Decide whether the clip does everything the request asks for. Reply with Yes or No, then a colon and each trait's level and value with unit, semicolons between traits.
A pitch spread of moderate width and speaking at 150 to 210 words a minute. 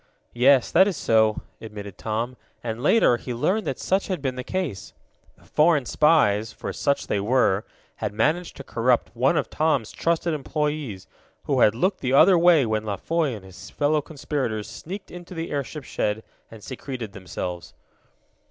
No: wide, 6.4 semitones; average, 170 wpm